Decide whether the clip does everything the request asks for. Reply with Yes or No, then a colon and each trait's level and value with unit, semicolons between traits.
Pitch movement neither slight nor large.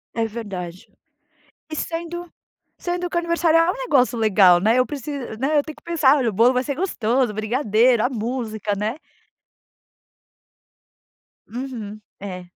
No: wide, 6.0 semitones